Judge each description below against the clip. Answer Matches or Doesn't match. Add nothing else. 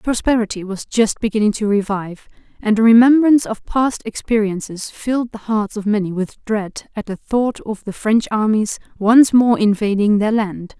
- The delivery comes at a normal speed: Matches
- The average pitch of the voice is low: Doesn't match